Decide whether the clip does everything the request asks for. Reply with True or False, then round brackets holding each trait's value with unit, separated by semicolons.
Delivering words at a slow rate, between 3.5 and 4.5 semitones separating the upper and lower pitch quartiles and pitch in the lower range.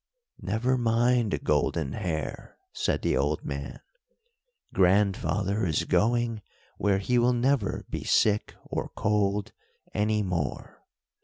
True (110 wpm; 4.2 semitones; 105 Hz)